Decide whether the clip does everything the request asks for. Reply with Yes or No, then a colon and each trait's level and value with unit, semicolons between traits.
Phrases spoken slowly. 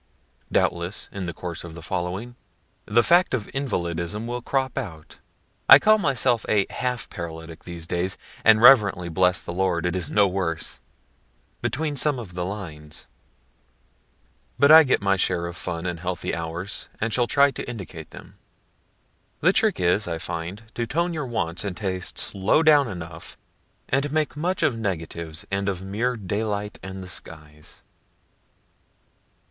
No: average, 160 wpm